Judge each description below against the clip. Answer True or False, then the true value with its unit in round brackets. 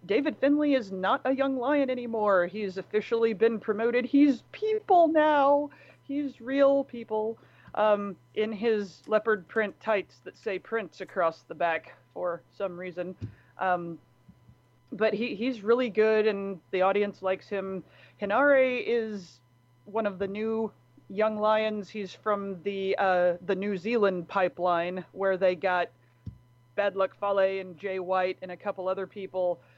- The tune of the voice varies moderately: True (3.8 semitones)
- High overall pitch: True (200 Hz)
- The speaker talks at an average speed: True (150 wpm)